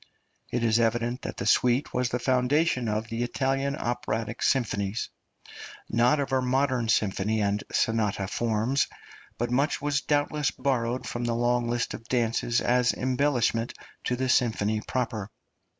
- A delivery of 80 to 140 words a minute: No, average, 150 wpm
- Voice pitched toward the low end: Yes, low, 120 Hz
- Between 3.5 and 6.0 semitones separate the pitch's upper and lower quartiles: No, narrow, 2.4 semitones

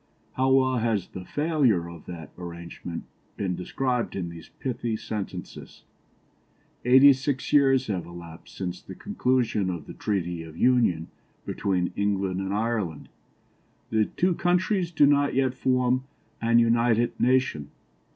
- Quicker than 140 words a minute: No, slow, 135 wpm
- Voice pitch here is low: Yes, low, 115 Hz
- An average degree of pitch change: No, wide, 6.4 semitones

